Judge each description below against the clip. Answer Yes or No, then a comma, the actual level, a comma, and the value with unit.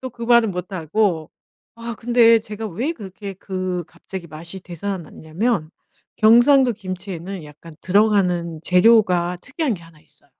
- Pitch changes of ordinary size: Yes, average, 4.8 semitones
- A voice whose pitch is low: No, high, 190 Hz